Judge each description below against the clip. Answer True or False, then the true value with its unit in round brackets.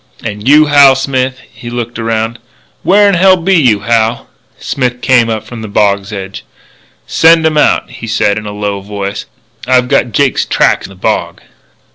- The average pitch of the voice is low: True (120 Hz)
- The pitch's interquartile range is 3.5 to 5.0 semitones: True (4.5 semitones)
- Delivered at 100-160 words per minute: False (185 wpm)